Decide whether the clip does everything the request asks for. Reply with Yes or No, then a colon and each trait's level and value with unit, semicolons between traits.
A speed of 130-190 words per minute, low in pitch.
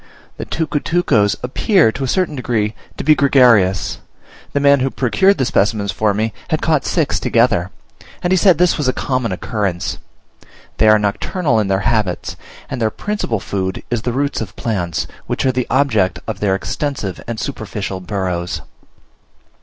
Yes: average, 170 wpm; low, 115 Hz